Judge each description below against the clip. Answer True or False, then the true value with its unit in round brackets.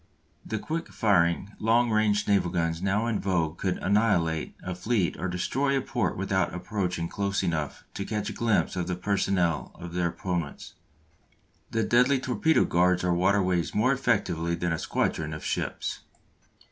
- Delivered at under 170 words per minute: True (160 wpm)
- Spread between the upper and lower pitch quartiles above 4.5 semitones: False (3.8 semitones)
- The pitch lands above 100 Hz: False (95 Hz)